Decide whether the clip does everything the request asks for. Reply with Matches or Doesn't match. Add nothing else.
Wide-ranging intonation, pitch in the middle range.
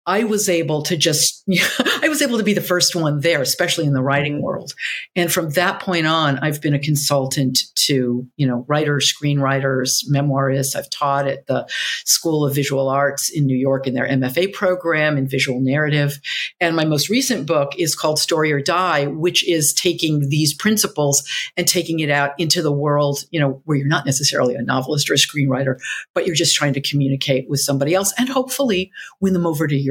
Doesn't match